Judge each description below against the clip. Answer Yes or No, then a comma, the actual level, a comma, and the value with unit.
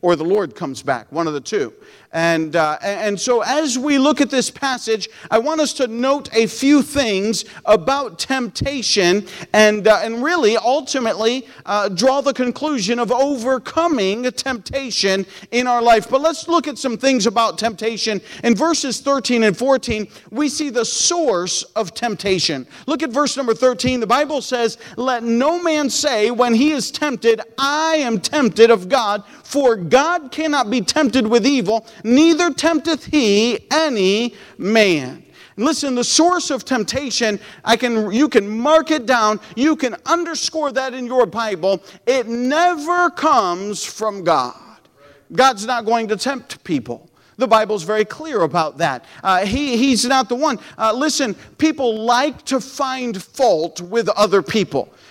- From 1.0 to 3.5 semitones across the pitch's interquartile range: No, average, 4.7 semitones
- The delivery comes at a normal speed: Yes, average, 160 wpm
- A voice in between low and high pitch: No, high, 245 Hz